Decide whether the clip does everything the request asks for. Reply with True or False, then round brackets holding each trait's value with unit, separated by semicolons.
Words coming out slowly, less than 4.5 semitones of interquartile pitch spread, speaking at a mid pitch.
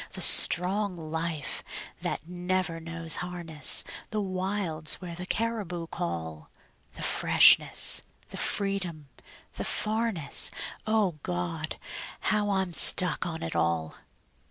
True (110 wpm; 3.7 semitones; 175 Hz)